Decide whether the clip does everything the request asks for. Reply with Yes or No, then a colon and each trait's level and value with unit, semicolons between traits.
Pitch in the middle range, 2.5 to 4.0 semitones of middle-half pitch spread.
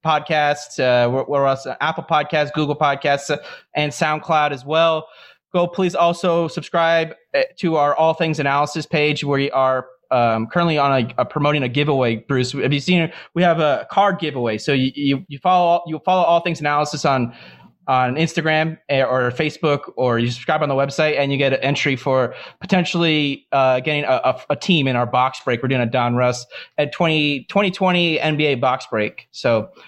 Yes: medium, 150 Hz; average, 3.6 semitones